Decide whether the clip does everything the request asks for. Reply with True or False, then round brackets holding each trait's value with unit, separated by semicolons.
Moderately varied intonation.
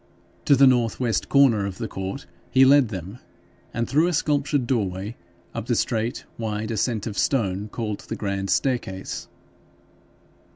True (4.7 semitones)